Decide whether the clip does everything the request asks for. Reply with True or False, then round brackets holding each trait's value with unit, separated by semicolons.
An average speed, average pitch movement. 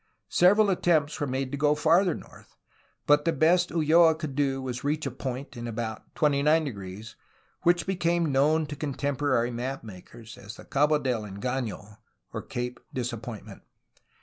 True (150 wpm; 4.3 semitones)